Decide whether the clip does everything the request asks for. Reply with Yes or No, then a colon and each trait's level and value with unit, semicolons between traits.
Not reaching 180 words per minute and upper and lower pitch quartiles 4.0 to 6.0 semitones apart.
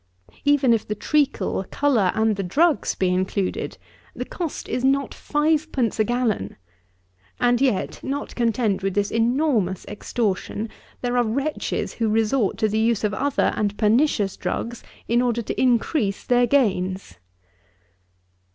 Yes: average, 140 wpm; average, 4.5 semitones